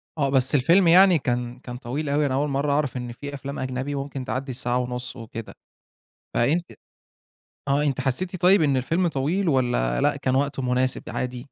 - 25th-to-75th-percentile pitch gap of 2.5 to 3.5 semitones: Yes, average, 2.8 semitones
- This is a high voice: No, low, 135 Hz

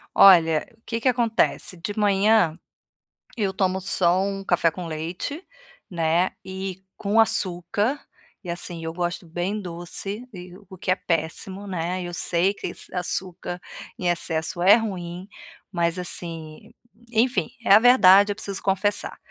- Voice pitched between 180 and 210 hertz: Yes, medium, 185 Hz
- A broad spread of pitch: No, average, 2.7 semitones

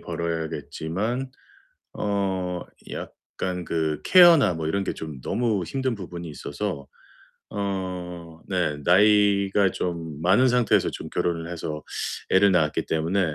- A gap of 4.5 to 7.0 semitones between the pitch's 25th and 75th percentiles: No, average, 3.8 semitones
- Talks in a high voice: No, very low, 90 Hz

